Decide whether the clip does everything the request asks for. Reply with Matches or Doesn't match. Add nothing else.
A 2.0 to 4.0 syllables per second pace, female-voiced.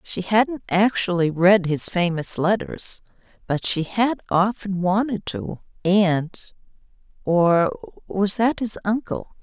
Matches